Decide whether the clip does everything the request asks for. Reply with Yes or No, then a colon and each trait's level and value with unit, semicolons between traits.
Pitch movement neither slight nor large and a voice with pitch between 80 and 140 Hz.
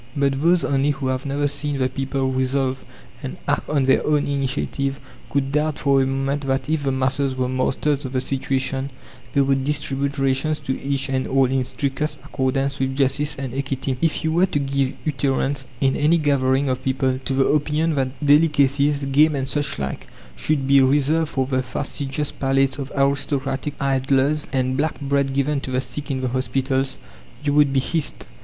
No: narrow, 1.5 semitones; low, 135 Hz